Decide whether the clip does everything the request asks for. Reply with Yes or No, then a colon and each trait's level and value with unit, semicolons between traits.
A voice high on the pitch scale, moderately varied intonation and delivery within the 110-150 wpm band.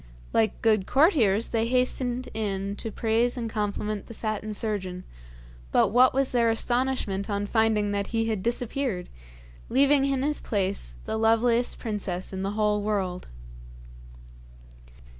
Yes: high, 220 Hz; average, 3.2 semitones; average, 140 wpm